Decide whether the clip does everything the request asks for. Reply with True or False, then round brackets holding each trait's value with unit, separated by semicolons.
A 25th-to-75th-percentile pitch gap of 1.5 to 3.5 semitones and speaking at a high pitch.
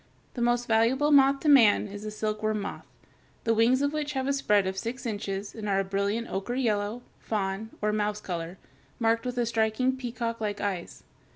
True (3.2 semitones; 220 Hz)